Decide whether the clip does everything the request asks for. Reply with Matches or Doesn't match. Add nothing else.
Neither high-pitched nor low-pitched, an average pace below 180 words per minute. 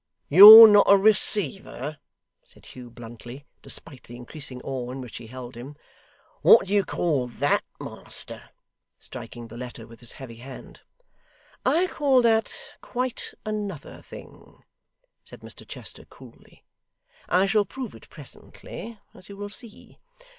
Matches